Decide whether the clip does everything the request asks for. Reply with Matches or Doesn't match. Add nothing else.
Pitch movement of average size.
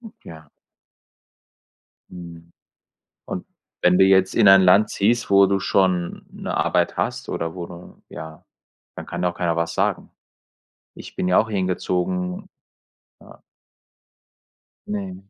Doesn't match